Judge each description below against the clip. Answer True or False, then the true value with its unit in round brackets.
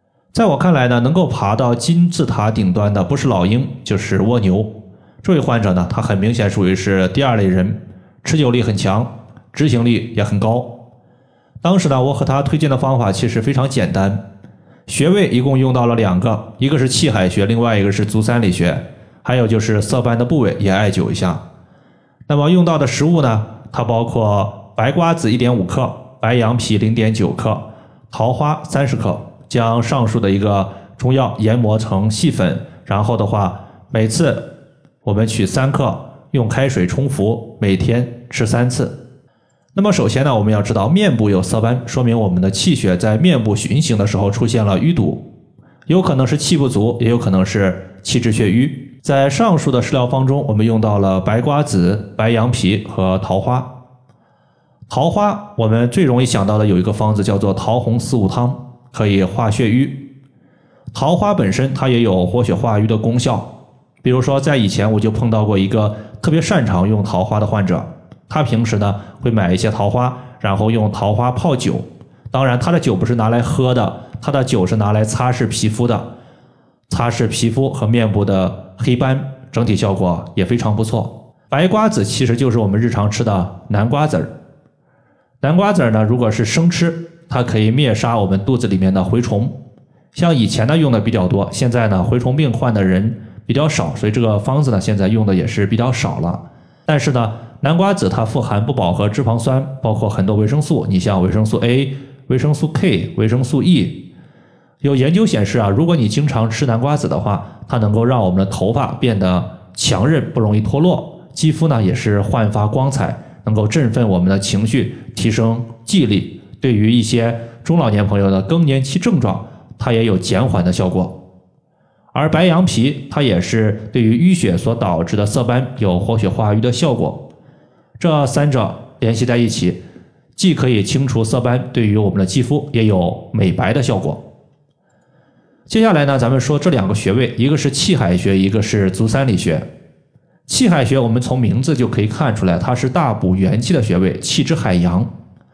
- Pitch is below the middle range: True (120 Hz)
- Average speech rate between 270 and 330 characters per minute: True (275 characters per minute)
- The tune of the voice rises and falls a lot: False (4.4 semitones)